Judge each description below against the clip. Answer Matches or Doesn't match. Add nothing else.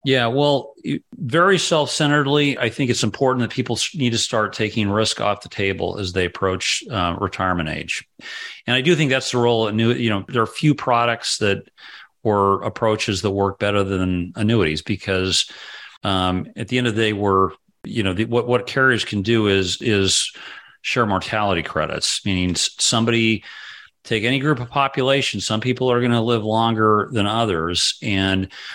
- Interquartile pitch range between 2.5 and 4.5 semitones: Matches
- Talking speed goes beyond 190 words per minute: Doesn't match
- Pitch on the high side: Doesn't match